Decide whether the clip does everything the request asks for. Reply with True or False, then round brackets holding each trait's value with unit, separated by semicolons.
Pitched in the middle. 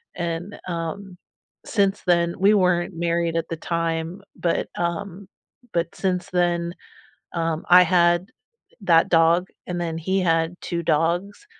True (175 Hz)